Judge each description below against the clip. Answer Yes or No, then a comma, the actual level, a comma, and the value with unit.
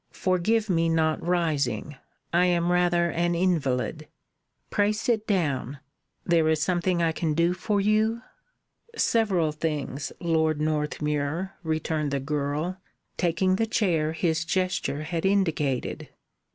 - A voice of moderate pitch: Yes, medium, 170 Hz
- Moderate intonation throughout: Yes, average, 3.2 semitones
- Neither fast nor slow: No, slow, 125 wpm